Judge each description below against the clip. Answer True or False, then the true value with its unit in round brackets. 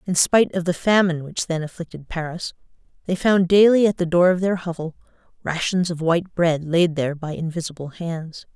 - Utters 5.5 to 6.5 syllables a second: True (5.6 syllables/s)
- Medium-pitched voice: True (170 Hz)